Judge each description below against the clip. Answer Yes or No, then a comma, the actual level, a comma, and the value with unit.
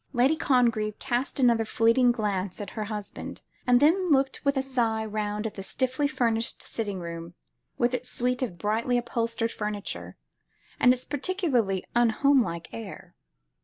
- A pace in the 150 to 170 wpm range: No, average, 140 wpm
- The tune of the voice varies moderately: Yes, average, 3.4 semitones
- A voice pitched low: No, high, 235 Hz